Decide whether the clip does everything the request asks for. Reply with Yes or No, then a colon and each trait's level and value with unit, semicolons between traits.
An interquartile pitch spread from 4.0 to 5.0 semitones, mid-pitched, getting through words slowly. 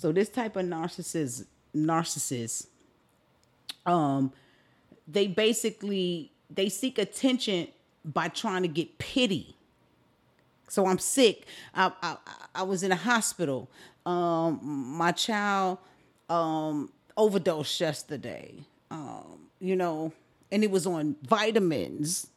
Yes: average, 4.7 semitones; medium, 180 Hz; slow, 110 wpm